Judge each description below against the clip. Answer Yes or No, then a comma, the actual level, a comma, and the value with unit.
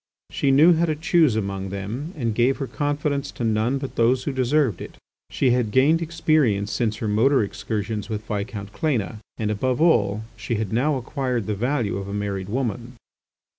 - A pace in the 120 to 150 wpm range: No, average, 185 wpm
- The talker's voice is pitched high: No, low, 120 Hz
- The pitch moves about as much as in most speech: Yes, average, 4.8 semitones